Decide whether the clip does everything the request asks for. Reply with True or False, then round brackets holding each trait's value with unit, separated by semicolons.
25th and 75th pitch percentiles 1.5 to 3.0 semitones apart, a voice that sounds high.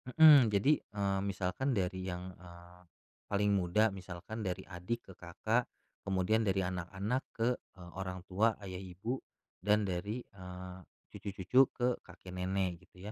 False (2.6 semitones; 95 Hz)